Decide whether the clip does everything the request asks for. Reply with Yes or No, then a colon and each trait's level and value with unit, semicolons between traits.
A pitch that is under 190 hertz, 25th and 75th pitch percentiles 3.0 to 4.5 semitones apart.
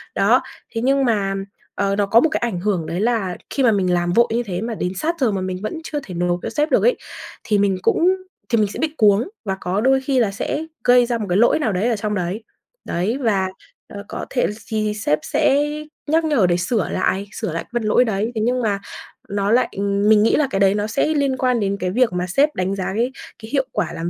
No: high, 215 Hz; average, 4.2 semitones